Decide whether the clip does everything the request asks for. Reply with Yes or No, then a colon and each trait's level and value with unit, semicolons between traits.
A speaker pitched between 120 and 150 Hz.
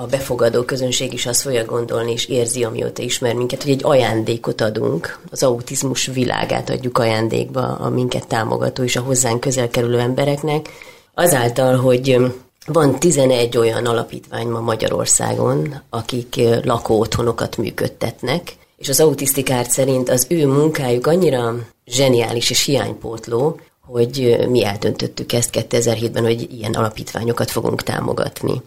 Yes: low, 125 Hz